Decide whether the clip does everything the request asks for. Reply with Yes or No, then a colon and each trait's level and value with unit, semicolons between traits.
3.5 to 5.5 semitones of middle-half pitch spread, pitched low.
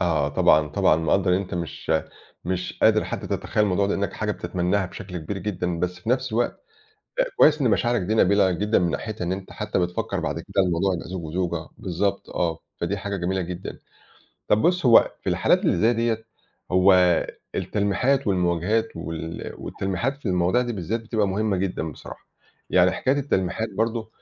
Yes: average, 3.9 semitones; very low, 95 Hz